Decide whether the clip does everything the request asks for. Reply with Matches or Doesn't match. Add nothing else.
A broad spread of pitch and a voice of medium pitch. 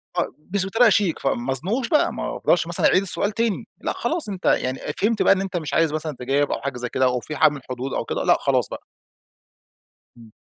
Matches